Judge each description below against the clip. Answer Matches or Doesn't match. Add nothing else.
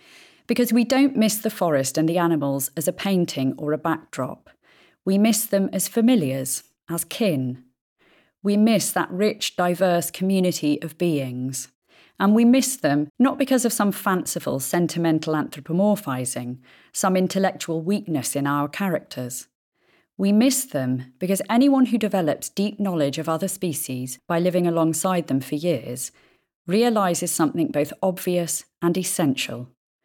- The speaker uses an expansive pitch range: Matches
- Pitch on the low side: Doesn't match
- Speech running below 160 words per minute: Matches